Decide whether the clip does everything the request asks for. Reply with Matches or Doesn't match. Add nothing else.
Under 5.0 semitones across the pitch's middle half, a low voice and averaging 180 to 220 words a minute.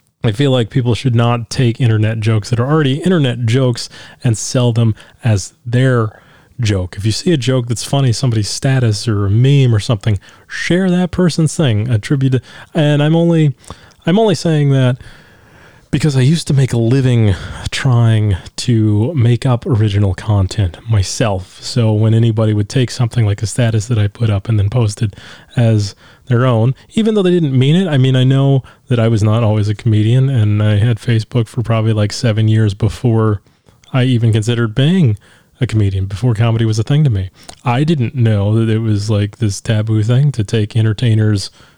Matches